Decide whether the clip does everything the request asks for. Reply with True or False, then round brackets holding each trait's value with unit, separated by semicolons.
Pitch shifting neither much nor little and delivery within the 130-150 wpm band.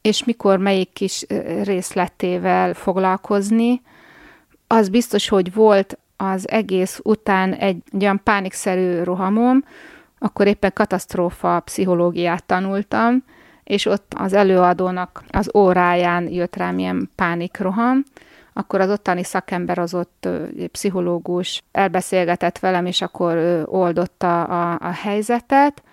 False (3.2 semitones; 110 wpm)